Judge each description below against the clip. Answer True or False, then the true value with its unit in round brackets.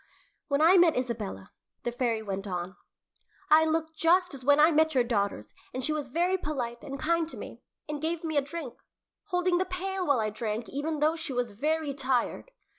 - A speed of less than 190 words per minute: False (200 wpm)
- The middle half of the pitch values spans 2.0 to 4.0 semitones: False (5.2 semitones)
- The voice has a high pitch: True (290 Hz)